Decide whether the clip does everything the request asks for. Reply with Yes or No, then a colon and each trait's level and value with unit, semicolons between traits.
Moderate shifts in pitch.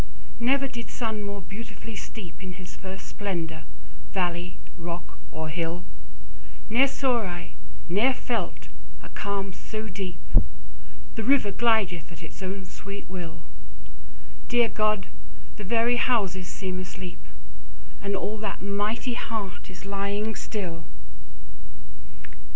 Yes: average, 3.5 semitones